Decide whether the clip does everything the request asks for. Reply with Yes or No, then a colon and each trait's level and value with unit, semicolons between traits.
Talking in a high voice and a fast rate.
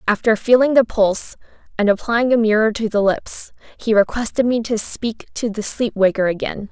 No: high, 220 Hz; average, 190 wpm